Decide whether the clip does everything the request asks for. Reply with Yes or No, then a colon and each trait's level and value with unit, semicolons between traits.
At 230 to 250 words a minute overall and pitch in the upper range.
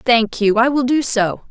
Yes: fast, 240 wpm; high, 240 Hz